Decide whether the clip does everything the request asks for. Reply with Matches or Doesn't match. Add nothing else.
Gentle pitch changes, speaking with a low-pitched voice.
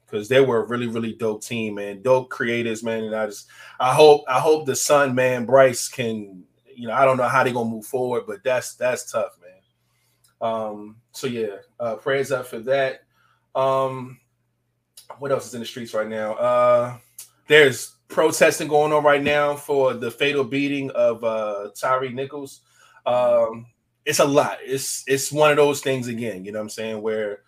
Doesn't match